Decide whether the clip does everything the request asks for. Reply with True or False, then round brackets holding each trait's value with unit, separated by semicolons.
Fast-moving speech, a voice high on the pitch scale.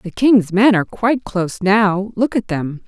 False (190 wpm; 200 Hz)